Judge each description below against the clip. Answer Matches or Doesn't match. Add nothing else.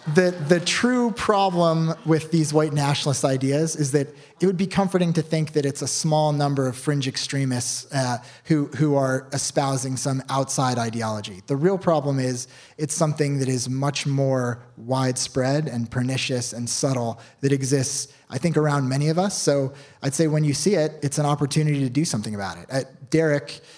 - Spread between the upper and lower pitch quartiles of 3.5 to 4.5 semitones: Doesn't match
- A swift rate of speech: Doesn't match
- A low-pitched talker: Doesn't match